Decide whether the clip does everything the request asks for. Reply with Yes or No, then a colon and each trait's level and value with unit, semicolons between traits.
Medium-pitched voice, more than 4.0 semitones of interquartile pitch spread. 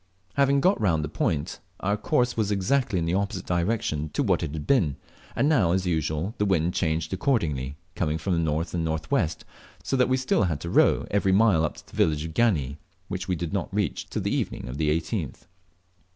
No: very low, 90 Hz; average, 4.8 semitones